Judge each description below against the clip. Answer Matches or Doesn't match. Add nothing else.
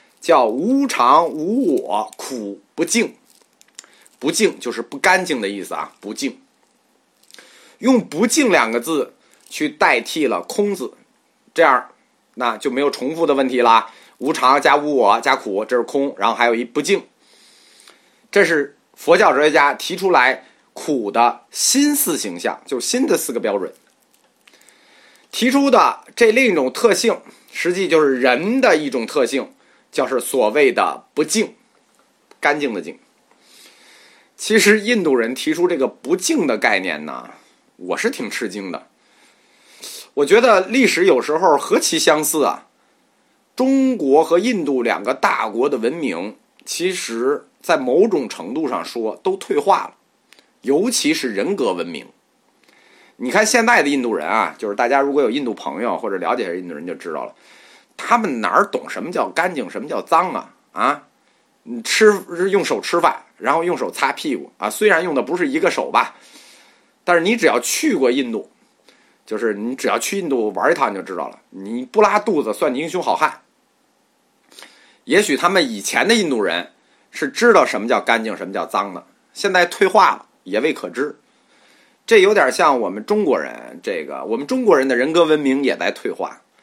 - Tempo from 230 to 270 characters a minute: Matches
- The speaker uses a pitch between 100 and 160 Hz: Doesn't match